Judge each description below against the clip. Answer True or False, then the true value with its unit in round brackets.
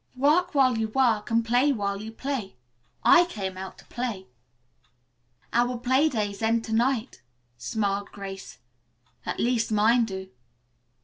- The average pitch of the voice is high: True (225 Hz)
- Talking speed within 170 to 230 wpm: False (140 wpm)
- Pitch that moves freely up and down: False (3.8 semitones)